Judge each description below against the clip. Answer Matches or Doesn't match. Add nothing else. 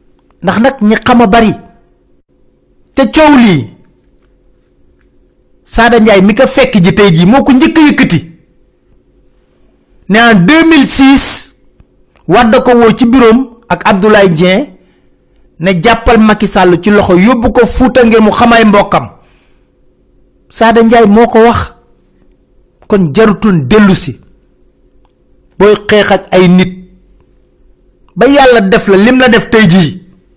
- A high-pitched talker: Matches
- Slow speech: Matches